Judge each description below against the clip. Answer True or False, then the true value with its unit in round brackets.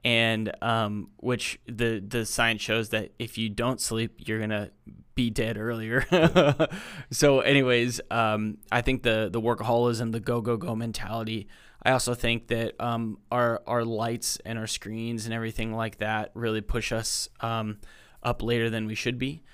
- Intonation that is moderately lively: False (1.5 semitones)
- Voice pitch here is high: False (115 Hz)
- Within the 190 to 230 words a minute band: False (170 wpm)